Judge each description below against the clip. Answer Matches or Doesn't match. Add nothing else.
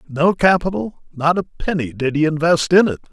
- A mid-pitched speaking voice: Matches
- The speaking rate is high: Doesn't match